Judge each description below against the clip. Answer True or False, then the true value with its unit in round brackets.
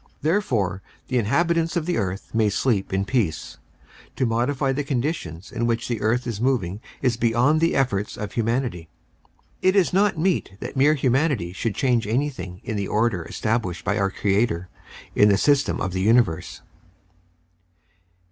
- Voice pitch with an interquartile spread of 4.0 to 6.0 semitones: True (5.6 semitones)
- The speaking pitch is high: False (115 Hz)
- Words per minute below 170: True (160 wpm)